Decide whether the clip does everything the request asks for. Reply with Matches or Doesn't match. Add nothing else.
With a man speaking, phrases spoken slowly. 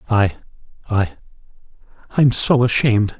Matches